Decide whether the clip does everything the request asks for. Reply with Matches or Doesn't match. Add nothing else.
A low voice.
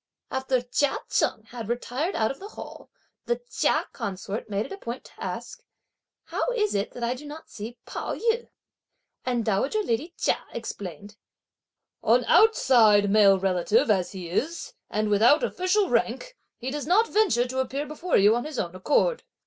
Doesn't match